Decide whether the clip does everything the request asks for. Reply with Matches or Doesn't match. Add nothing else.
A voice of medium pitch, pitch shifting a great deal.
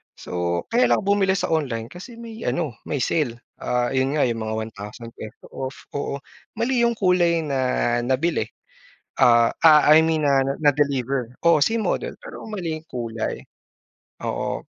Matches